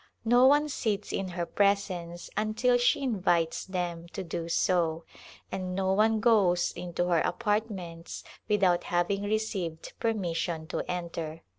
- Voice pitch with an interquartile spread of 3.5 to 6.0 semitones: Yes, average, 3.8 semitones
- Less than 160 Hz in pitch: No, medium, 185 Hz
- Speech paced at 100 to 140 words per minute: Yes, slow, 135 wpm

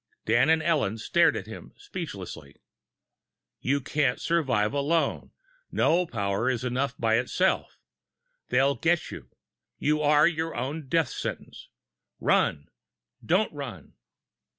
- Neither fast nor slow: No, slow, 120 wpm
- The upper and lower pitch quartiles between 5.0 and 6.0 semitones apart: Yes, wide, 5.4 semitones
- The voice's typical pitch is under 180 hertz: Yes, medium, 140 Hz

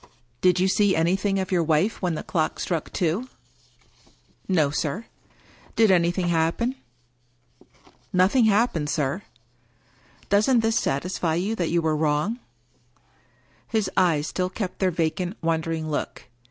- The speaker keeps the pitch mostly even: No, average, 3.7 semitones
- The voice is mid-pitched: Yes, medium, 175 Hz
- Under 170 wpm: Yes, average, 160 wpm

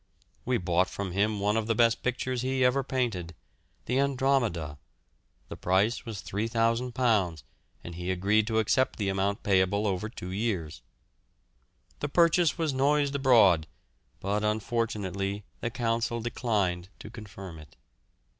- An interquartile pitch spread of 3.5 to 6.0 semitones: Yes, average, 4.5 semitones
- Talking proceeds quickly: No, slow, 135 wpm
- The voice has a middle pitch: No, low, 110 Hz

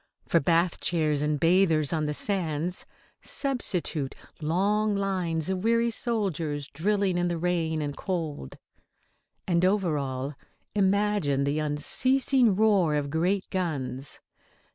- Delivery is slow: Yes, slow, 120 wpm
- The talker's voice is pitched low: No, medium, 170 Hz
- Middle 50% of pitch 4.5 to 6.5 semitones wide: Yes, average, 4.8 semitones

